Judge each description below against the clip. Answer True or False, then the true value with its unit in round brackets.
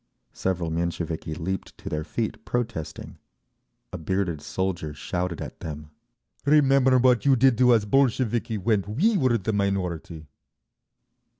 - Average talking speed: False (130 wpm)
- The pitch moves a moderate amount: False (6.4 semitones)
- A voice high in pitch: False (100 Hz)